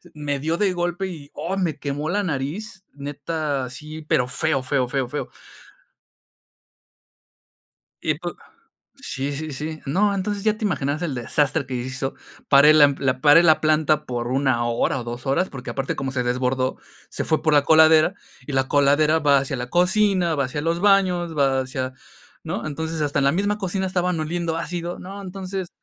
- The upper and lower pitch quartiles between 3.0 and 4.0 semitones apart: No, average, 4.4 semitones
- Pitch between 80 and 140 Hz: No, medium, 150 Hz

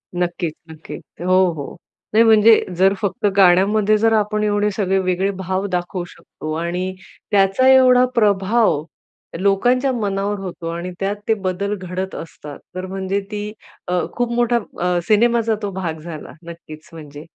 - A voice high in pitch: Yes, high, 195 Hz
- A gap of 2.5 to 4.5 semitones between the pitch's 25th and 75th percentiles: Yes, average, 3.0 semitones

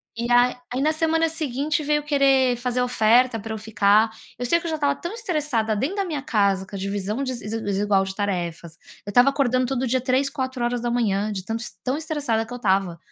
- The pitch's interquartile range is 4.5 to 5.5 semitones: Yes, average, 5.0 semitones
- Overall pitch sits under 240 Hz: No, high, 245 Hz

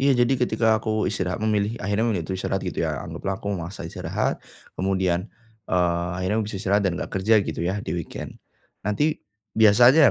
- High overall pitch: No, low, 100 Hz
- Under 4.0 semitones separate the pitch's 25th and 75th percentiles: Yes, average, 2.8 semitones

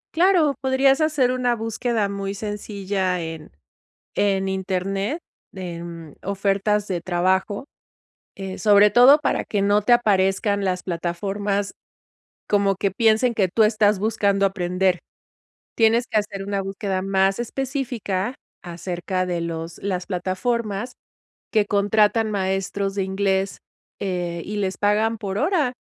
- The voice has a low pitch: No, high, 200 Hz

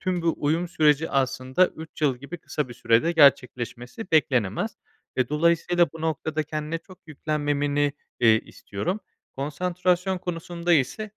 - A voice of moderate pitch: Yes, medium, 155 Hz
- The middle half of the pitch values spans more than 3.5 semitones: Yes, average, 3.9 semitones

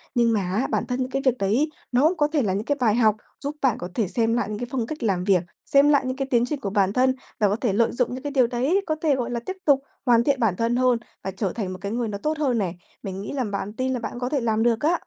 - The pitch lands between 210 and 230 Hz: No, high, 240 Hz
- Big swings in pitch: No, average, 4.2 semitones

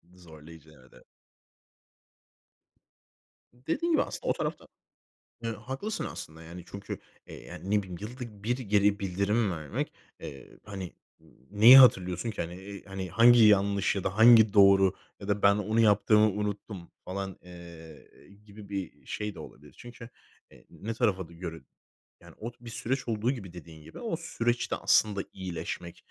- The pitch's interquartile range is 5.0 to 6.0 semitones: No, average, 3.9 semitones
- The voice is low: Yes, low, 100 Hz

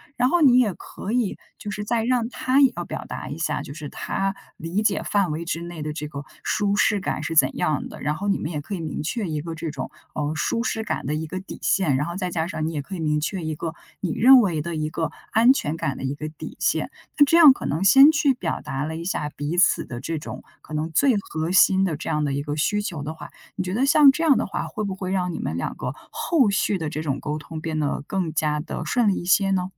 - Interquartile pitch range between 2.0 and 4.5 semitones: No, average, 5.3 semitones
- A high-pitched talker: No, medium, 170 Hz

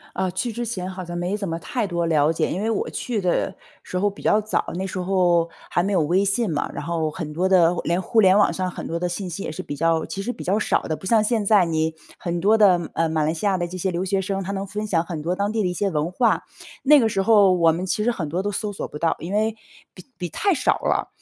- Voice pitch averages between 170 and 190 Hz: Yes, medium, 185 Hz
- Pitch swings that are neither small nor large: Yes, average, 3.3 semitones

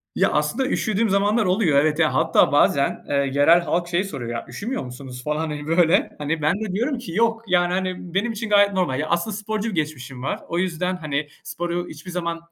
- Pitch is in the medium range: Yes, medium, 175 Hz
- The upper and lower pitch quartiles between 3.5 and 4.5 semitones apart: No, average, 5.0 semitones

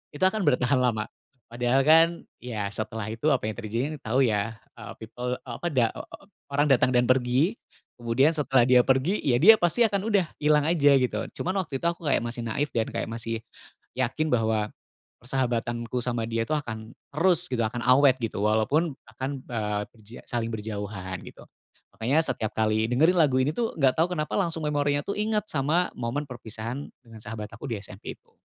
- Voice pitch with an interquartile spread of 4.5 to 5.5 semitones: Yes, average, 4.8 semitones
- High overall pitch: No, low, 125 Hz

